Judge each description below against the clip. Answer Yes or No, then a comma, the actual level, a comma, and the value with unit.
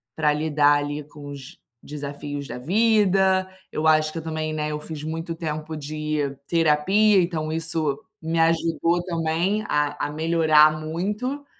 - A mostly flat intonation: Yes, narrow, 2.1 semitones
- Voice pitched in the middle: Yes, medium, 155 Hz